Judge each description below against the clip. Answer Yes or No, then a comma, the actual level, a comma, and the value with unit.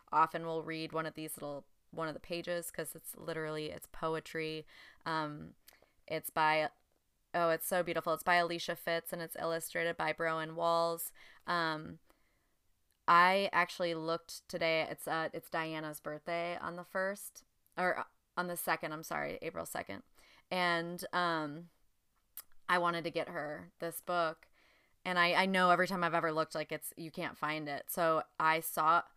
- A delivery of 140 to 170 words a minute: Yes, average, 165 wpm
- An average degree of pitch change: No, narrow, 1.5 semitones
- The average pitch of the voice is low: No, medium, 165 Hz